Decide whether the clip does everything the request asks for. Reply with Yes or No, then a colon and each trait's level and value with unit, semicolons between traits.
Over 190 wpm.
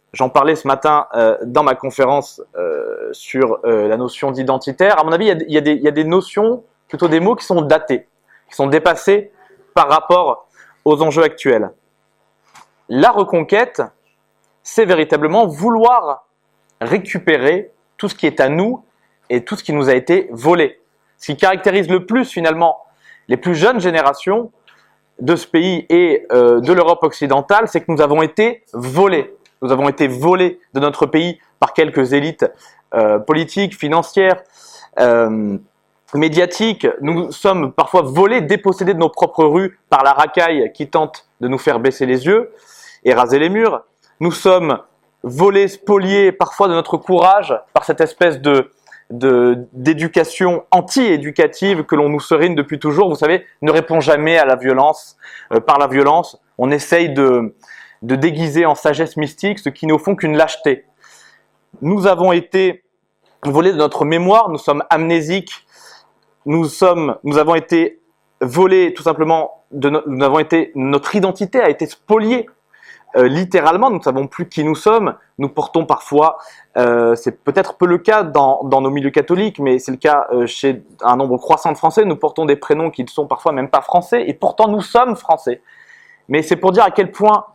No: average, 175 wpm